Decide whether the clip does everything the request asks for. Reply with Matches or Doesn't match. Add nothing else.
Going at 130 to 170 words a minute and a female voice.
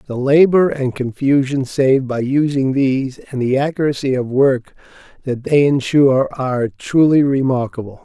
Doesn't match